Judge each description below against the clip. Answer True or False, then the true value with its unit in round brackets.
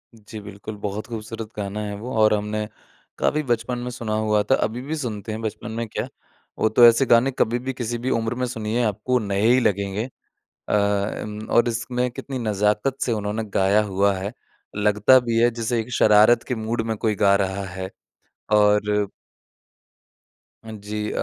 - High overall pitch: False (110 Hz)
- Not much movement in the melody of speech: True (2.3 semitones)